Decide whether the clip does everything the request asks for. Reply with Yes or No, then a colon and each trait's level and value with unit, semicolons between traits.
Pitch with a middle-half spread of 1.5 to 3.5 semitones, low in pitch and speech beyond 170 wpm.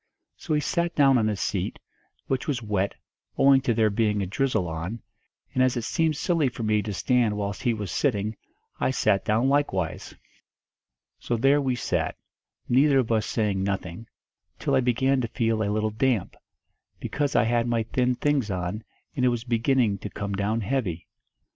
No: average, 4.1 semitones; low, 115 Hz; average, 185 wpm